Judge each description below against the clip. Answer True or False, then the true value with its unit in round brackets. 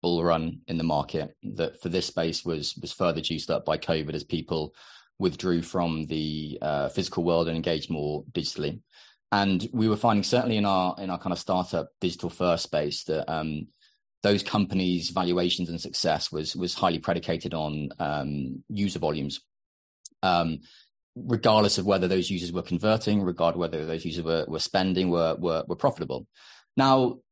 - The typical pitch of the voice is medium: False (85 Hz)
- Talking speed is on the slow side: False (170 wpm)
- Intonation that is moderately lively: True (3.2 semitones)